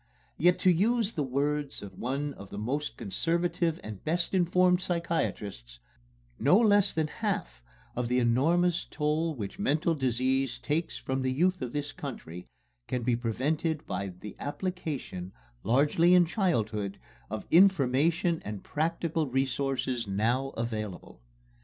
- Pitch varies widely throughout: Yes, wide, 6.3 semitones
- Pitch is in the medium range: Yes, medium, 145 Hz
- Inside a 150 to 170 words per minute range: No, slow, 135 wpm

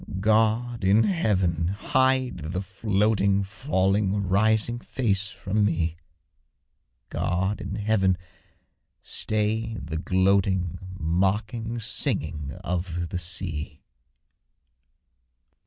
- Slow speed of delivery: Yes, slow, 85 wpm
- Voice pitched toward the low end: Yes, low, 100 Hz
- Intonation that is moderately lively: Yes, average, 3.3 semitones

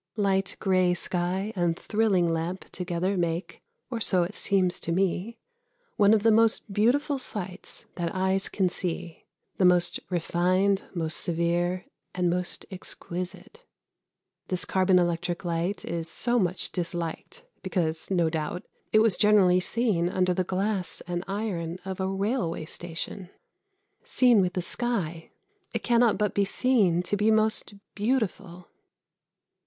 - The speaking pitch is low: No, medium, 185 Hz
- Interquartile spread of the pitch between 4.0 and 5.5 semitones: No, average, 3.0 semitones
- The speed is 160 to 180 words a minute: No, average, 140 wpm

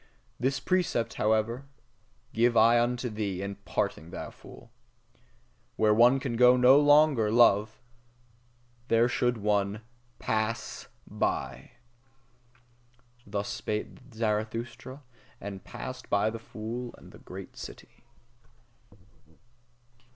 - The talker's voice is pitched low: Yes, low, 115 Hz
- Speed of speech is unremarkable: No, slow, 100 wpm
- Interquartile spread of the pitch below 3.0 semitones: Yes, narrow, 2.6 semitones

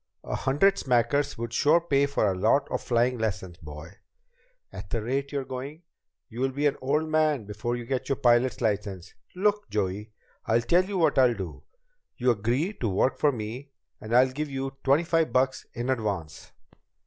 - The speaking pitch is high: No, low, 130 Hz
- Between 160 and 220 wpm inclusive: Yes, average, 185 wpm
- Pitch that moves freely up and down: No, average, 4.5 semitones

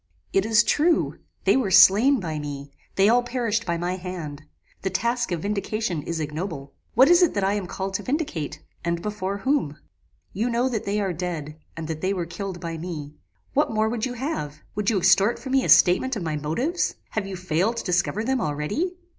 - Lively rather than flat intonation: Yes, wide, 5.7 semitones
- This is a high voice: Yes, high, 195 Hz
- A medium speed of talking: No, fast, 210 wpm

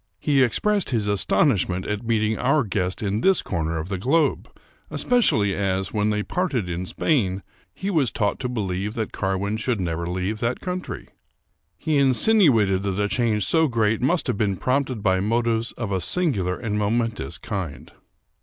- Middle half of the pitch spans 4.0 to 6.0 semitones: Yes, average, 5.1 semitones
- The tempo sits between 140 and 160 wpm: No, average, 175 wpm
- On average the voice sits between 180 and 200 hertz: No, low, 110 Hz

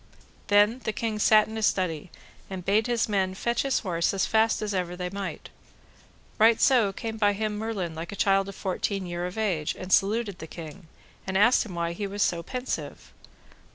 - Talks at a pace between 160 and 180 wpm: No, average, 200 wpm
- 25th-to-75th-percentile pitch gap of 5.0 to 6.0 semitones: No, average, 3.3 semitones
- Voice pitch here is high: Yes, high, 200 Hz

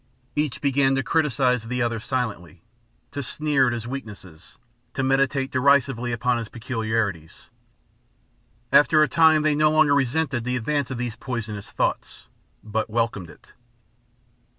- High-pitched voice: No, low, 125 Hz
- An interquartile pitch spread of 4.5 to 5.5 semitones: No, average, 3.8 semitones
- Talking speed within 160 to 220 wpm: No, average, 140 wpm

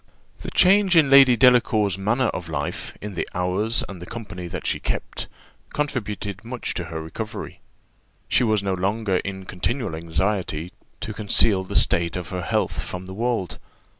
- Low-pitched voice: Yes, low, 100 Hz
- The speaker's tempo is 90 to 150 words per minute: No, average, 165 wpm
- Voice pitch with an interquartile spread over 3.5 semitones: Yes, average, 4.5 semitones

